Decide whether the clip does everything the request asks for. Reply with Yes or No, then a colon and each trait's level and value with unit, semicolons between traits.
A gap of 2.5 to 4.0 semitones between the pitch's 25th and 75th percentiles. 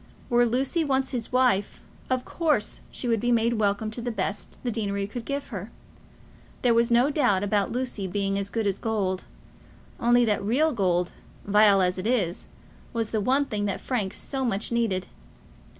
Yes: average, 3.7 semitones